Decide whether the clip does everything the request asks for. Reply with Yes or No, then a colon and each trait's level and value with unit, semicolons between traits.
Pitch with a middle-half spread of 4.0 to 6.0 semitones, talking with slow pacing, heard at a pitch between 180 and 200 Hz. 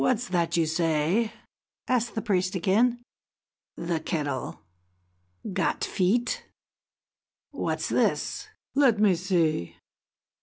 Yes: wide, 5.6 semitones; slow, 105 wpm; medium, 185 Hz